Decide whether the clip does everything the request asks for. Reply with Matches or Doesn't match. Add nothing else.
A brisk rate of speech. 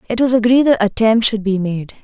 Matches